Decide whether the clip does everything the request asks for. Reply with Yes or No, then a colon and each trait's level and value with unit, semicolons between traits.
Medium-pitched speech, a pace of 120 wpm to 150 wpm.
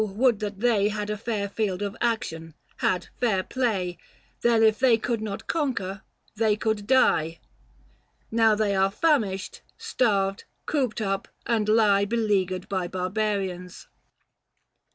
No: high, 210 Hz; slow, 135 wpm